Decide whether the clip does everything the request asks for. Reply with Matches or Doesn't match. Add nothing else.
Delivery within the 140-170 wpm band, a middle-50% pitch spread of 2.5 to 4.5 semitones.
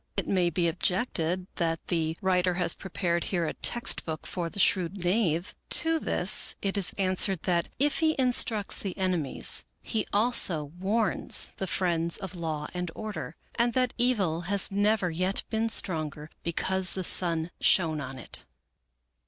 Matches